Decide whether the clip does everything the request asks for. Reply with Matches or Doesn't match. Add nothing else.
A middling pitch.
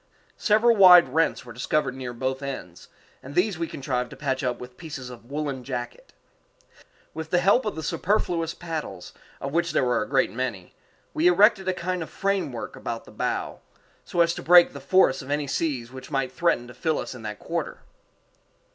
Matches